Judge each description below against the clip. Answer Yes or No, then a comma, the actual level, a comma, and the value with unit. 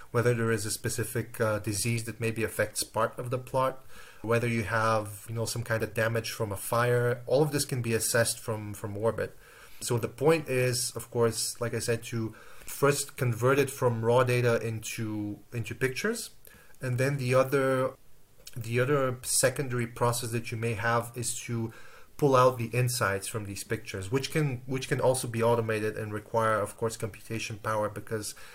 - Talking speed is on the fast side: No, average, 185 wpm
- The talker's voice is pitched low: Yes, low, 115 Hz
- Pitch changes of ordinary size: No, narrow, 2.1 semitones